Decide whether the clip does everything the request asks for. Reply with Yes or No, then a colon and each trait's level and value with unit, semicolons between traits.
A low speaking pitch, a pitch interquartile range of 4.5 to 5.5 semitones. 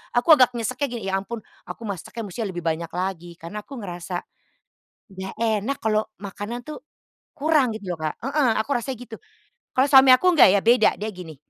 No: high, 220 Hz; average, 5.0 semitones